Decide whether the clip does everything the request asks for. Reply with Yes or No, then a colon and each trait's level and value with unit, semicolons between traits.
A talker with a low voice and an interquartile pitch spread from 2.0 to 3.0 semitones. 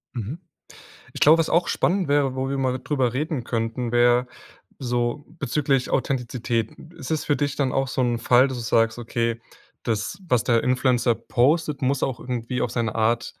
Yes: low, 125 Hz; average, 2.7 semitones